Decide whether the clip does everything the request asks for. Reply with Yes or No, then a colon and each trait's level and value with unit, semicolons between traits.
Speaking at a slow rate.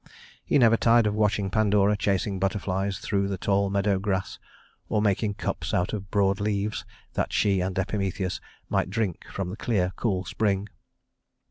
No: average, 160 wpm